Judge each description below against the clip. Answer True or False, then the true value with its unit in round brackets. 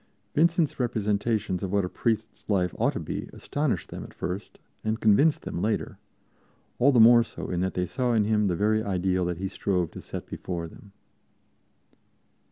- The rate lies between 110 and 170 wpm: False (180 wpm)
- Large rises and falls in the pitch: False (4.0 semitones)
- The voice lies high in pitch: False (105 Hz)